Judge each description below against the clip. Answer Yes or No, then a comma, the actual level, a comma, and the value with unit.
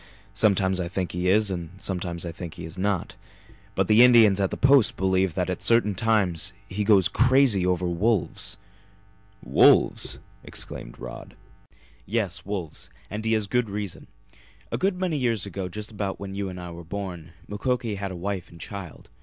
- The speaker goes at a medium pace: Yes, average, 180 wpm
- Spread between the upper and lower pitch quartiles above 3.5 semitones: No, average, 3.2 semitones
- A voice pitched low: Yes, low, 100 Hz